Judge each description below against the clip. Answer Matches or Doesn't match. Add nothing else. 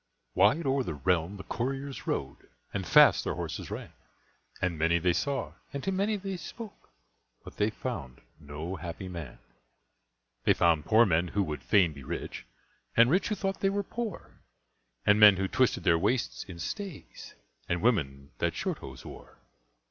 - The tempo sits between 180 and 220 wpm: Doesn't match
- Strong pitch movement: Matches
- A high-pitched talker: Doesn't match